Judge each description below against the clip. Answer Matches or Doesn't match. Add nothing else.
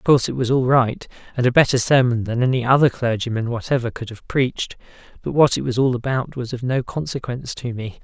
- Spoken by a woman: Doesn't match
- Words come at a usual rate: Doesn't match